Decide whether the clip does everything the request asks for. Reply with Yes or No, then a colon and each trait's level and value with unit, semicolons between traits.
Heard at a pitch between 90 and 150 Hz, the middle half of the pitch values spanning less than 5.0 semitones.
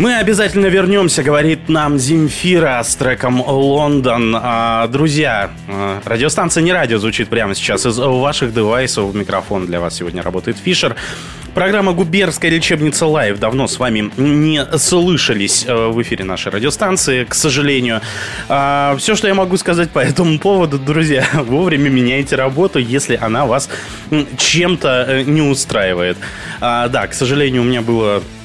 No: medium, 140 Hz; wide, 5.6 semitones